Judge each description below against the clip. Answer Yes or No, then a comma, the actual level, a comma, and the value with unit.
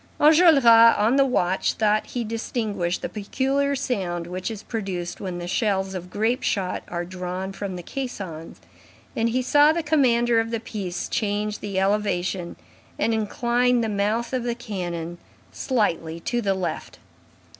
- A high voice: Yes, high, 210 Hz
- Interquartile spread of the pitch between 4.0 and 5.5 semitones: Yes, average, 4.5 semitones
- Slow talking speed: No, average, 155 wpm